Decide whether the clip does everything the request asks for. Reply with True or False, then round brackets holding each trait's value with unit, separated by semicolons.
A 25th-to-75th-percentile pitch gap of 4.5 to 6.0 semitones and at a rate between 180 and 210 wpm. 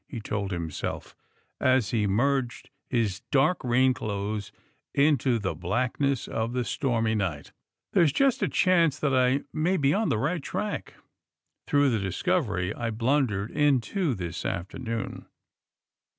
False (5.5 semitones; 140 wpm)